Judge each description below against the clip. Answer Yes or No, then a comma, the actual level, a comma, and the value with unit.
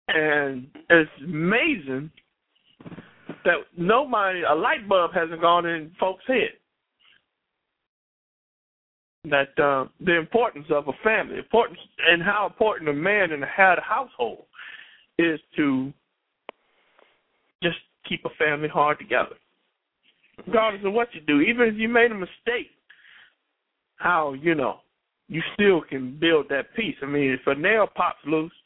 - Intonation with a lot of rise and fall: Yes, wide, 6.7 semitones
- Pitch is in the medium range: Yes, medium, 170 Hz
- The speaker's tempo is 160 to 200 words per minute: No, slow, 135 wpm